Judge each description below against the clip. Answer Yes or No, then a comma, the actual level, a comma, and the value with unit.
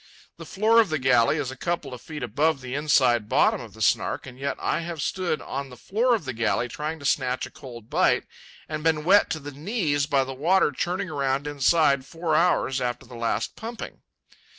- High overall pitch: No, medium, 145 Hz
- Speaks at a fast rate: Yes, fast, 215 wpm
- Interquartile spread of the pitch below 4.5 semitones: Yes, average, 4.1 semitones